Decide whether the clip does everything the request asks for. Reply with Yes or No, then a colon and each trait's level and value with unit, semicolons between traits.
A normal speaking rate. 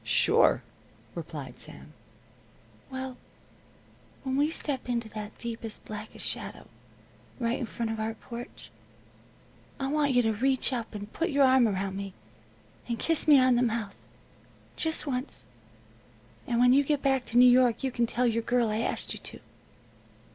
Yes: average, 160 wpm